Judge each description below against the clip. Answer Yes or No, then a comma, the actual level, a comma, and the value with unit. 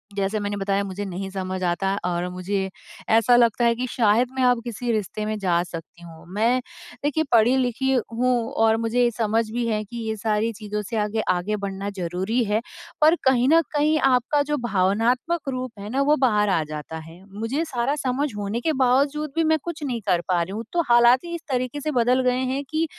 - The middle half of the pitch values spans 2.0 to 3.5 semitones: No, average, 4.3 semitones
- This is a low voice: No, high, 225 Hz